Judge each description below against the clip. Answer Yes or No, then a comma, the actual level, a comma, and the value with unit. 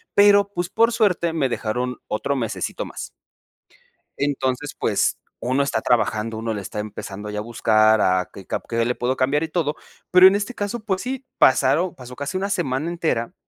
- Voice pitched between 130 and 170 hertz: Yes, low, 135 Hz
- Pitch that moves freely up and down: Yes, wide, 8.1 semitones